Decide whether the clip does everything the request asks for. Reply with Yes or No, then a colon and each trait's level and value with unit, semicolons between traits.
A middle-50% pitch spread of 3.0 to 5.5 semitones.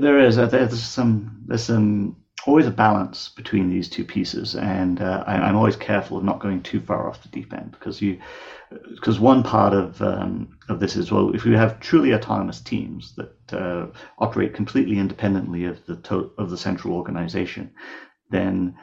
Yes: average, 3.7 semitones